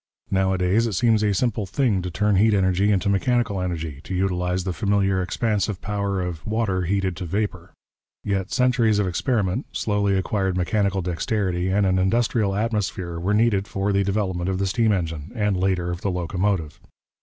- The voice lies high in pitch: No, very low, 95 Hz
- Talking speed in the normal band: Yes, average, 175 wpm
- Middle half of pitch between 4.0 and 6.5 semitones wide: No, narrow, 2.5 semitones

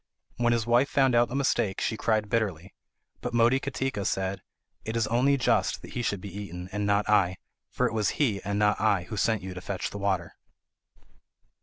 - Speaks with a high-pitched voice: No, low, 105 Hz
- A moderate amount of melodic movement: Yes, average, 3.3 semitones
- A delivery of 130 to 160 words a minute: No, average, 200 wpm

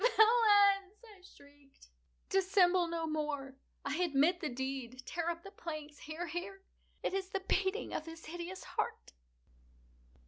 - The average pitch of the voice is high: Yes, very high, 345 Hz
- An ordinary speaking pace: No, slow, 125 wpm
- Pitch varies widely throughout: No, average, 4.5 semitones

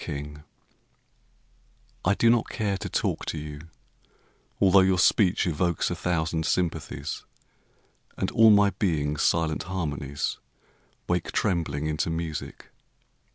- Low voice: Yes, very low, 85 Hz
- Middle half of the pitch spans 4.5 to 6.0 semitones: No, average, 3.8 semitones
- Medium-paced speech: No, slow, 115 wpm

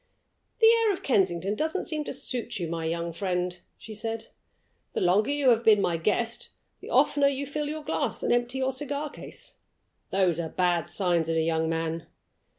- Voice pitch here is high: Yes, high, 210 Hz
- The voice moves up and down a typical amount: No, wide, 8.5 semitones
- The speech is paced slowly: No, average, 190 wpm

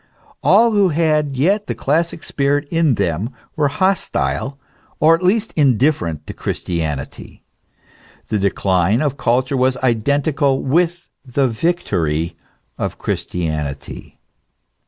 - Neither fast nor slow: No, slow, 115 wpm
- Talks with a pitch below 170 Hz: Yes, medium, 140 Hz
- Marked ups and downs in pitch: Yes, wide, 8.1 semitones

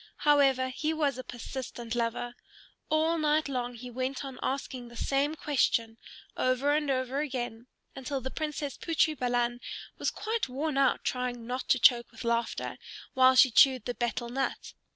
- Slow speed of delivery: No, average, 165 wpm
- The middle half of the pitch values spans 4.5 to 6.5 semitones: No, average, 2.8 semitones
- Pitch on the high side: Yes, very high, 260 Hz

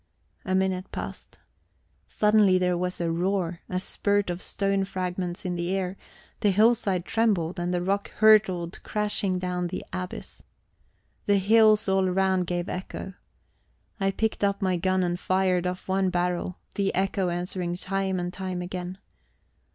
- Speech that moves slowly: No, average, 150 wpm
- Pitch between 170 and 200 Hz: Yes, medium, 185 Hz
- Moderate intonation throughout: No, narrow, 1.5 semitones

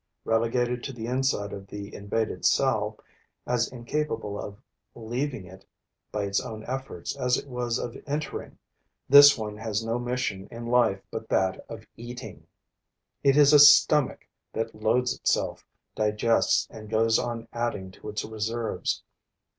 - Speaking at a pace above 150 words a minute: No, average, 145 wpm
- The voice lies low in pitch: Yes, low, 115 Hz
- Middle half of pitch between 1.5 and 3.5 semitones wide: Yes, average, 2.7 semitones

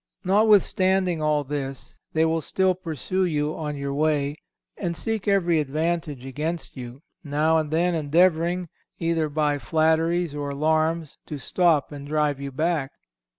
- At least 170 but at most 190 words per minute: No, average, 145 wpm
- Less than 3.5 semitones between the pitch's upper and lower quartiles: Yes, average, 2.9 semitones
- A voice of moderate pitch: Yes, medium, 155 Hz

